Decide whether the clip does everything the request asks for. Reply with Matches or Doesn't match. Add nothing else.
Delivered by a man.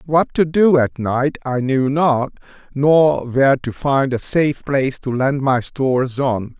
Matches